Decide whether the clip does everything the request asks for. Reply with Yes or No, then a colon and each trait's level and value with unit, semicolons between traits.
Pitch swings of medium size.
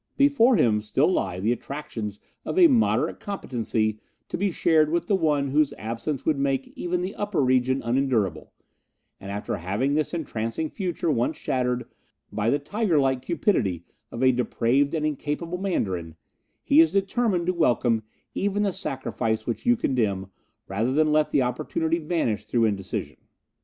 No: wide, 6.9 semitones